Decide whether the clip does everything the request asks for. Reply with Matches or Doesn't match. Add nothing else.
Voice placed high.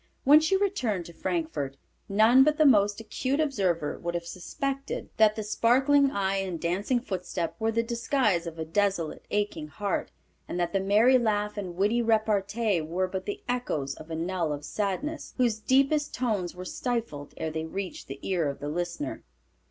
Matches